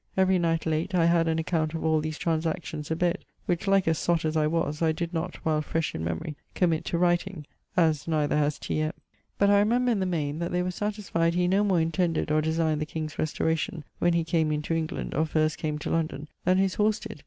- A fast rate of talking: Yes, fast, 235 wpm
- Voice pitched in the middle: Yes, medium, 165 Hz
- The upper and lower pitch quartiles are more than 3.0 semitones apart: No, narrow, 2.4 semitones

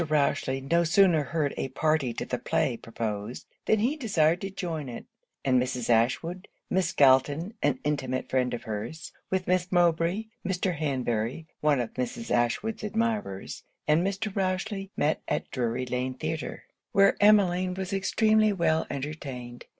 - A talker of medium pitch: Yes, medium, 155 Hz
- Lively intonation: Yes, wide, 6.6 semitones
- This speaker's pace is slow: No, average, 150 wpm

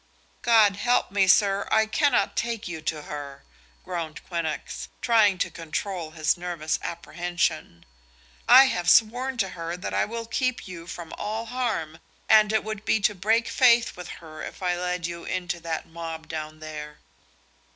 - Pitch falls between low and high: Yes, medium, 180 Hz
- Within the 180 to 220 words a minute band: No, average, 165 wpm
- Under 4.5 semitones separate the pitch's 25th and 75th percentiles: No, average, 5.0 semitones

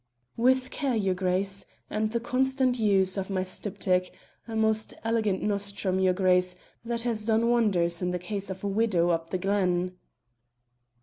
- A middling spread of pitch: Yes, average, 3.5 semitones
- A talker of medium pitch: No, high, 200 Hz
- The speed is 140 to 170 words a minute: Yes, average, 165 wpm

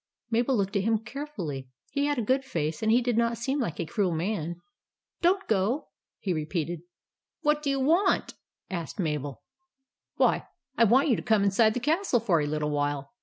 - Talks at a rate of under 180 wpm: No, average, 200 wpm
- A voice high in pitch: Yes, high, 220 Hz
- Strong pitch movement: Yes, wide, 8.2 semitones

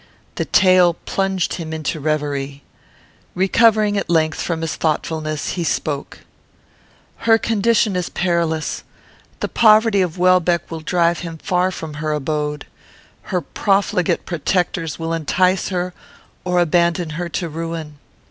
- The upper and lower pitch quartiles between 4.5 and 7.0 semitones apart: No, average, 2.8 semitones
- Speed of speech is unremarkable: No, slow, 130 wpm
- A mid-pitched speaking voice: Yes, medium, 170 Hz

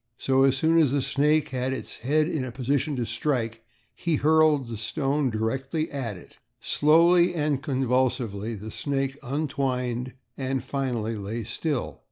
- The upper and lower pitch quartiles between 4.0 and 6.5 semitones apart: No, average, 3.6 semitones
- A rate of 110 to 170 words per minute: Yes, average, 155 wpm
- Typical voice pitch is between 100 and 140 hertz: Yes, low, 135 Hz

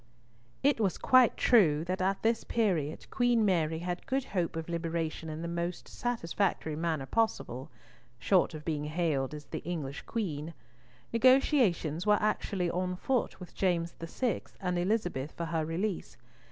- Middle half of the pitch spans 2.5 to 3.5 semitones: No, average, 4.7 semitones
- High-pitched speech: No, medium, 175 Hz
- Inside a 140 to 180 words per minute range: Yes, average, 145 wpm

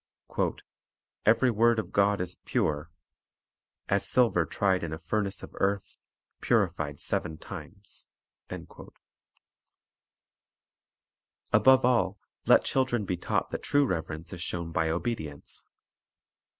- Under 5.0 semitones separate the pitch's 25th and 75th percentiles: No, wide, 5.5 semitones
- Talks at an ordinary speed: No, slow, 110 wpm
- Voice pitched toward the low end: Yes, very low, 95 Hz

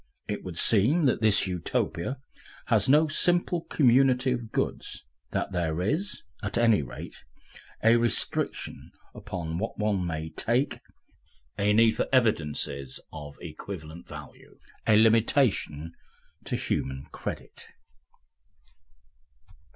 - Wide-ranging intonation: Yes, wide, 6.8 semitones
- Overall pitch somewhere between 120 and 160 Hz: No, low, 105 Hz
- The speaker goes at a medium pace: No, slow, 110 wpm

